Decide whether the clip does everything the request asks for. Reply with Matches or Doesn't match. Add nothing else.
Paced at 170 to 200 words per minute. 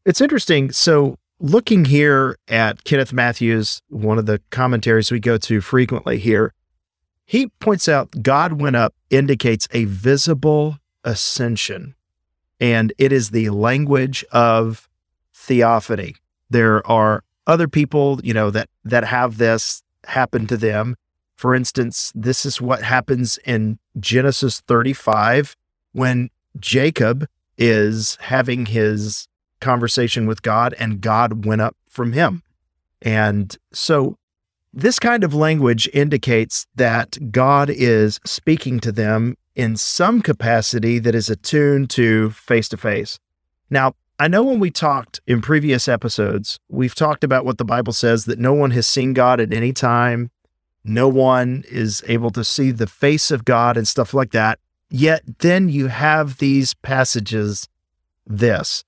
Doesn't match